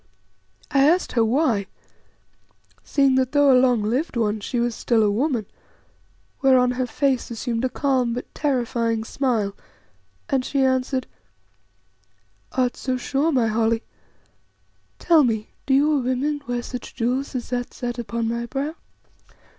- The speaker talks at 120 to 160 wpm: Yes, average, 145 wpm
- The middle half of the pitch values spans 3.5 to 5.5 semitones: No, narrow, 2.6 semitones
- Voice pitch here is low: No, very high, 250 Hz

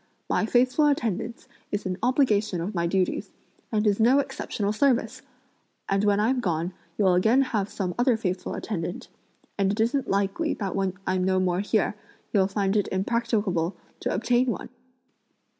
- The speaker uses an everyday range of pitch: Yes, average, 3.8 semitones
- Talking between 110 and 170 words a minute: Yes, average, 160 wpm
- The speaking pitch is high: Yes, high, 205 Hz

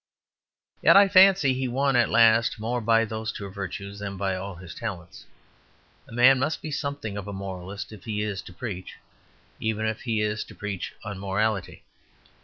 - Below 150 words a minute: No, average, 180 wpm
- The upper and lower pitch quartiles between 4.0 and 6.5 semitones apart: No, average, 3.5 semitones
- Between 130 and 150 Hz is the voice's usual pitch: No, low, 110 Hz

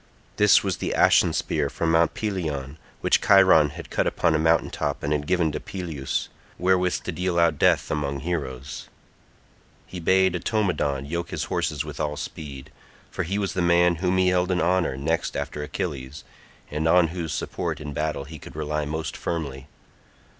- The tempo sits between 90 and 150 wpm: No, average, 180 wpm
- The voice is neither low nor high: No, very low, 80 Hz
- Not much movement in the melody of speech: No, average, 3.5 semitones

